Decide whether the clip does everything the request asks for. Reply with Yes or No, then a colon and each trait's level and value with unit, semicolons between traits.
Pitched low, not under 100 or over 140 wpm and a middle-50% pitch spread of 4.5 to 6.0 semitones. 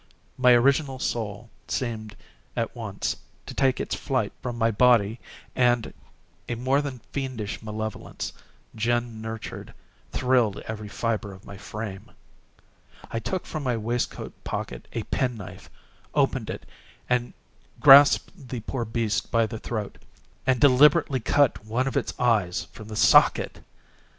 No: low, 115 Hz; slow, 135 wpm; average, 3.0 semitones